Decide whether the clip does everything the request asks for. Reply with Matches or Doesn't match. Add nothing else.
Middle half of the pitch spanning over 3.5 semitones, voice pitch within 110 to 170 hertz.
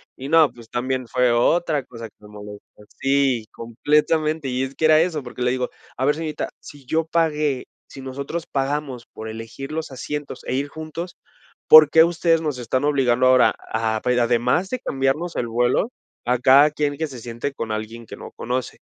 Matches